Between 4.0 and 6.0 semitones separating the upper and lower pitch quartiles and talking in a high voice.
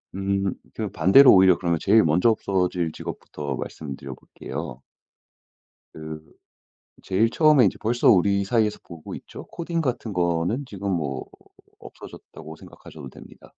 No: wide, 5.5 semitones; very low, 95 Hz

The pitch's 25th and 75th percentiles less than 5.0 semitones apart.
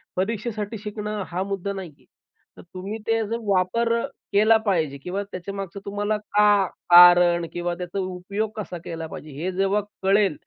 Yes: average, 2.7 semitones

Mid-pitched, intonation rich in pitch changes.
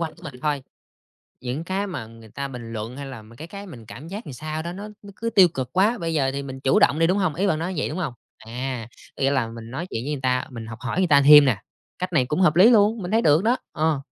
Yes: medium, 150 Hz; wide, 6.1 semitones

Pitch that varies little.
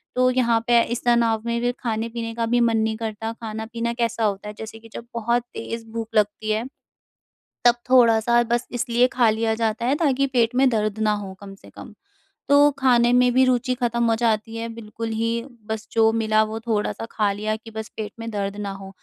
Yes: narrow, 1.6 semitones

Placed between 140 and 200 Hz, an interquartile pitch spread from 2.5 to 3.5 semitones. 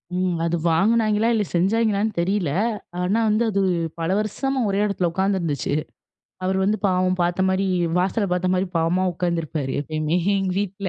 Yes: high, 190 Hz; average, 3.0 semitones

